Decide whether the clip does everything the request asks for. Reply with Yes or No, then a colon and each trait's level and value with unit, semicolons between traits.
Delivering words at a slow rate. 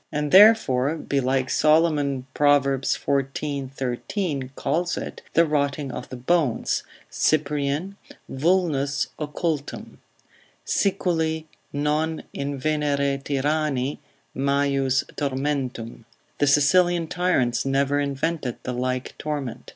Yes: slow, 95 wpm